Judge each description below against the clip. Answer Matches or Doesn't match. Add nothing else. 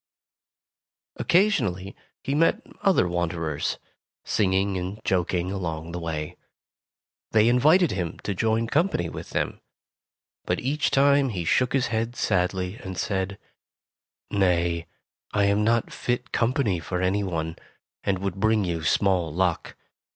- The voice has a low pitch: Matches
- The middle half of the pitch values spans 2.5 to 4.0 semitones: Doesn't match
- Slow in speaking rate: Matches